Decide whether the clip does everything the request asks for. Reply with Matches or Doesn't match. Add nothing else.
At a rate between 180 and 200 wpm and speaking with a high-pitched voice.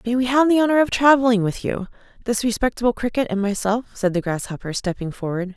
Matches